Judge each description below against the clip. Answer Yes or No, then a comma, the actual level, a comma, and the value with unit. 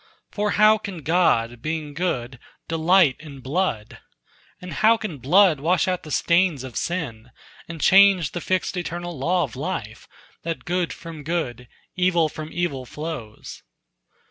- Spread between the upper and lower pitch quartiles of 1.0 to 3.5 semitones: No, average, 4.8 semitones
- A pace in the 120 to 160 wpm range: Yes, average, 145 wpm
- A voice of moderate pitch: Yes, medium, 165 Hz